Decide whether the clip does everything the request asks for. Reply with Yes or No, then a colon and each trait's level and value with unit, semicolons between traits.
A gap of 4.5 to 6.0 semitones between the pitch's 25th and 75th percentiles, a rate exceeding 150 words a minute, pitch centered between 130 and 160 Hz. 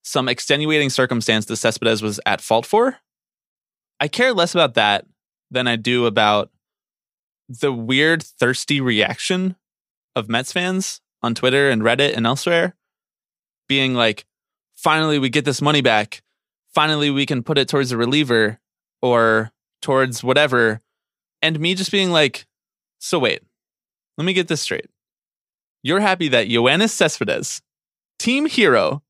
No: average, 5.2 semitones; average, 140 wpm; low, 135 Hz